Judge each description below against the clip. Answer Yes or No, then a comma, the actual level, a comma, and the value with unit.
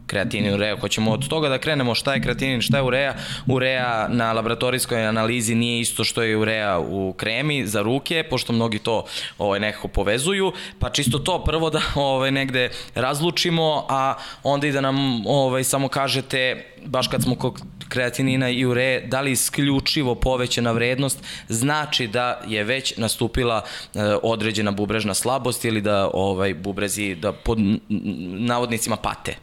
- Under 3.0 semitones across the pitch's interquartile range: No, average, 3.4 semitones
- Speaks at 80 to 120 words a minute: No, average, 155 wpm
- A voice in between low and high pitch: No, low, 125 Hz